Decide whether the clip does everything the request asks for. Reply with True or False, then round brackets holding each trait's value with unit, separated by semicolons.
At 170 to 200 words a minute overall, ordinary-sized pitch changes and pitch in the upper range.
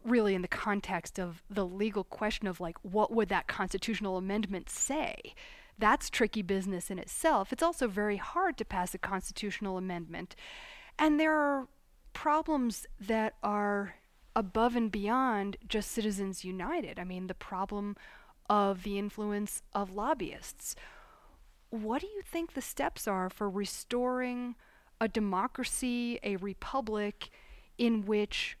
False (140 wpm; 4.0 semitones; 210 Hz)